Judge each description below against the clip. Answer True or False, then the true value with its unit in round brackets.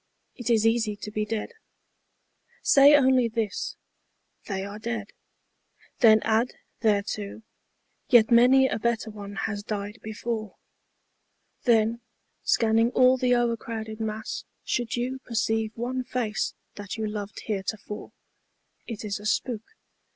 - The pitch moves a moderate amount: False (2.1 semitones)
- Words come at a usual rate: False (130 wpm)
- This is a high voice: True (225 Hz)